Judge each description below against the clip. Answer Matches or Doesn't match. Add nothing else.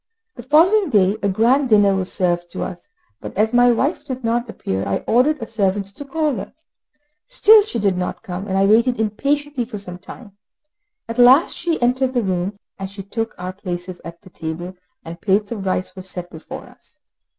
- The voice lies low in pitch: Doesn't match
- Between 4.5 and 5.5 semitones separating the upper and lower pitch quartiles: Matches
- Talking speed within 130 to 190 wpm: Doesn't match